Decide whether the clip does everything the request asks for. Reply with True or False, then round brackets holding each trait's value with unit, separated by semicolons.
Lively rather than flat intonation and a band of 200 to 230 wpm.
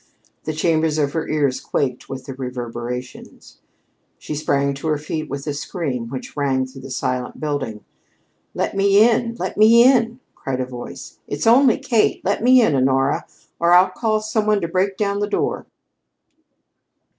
False (7.9 semitones; 170 wpm)